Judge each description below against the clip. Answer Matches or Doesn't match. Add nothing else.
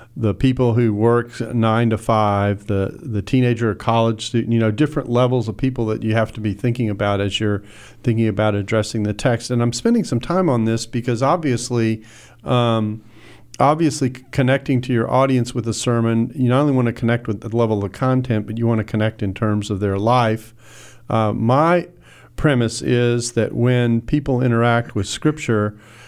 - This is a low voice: Matches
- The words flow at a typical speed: Matches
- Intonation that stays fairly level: Matches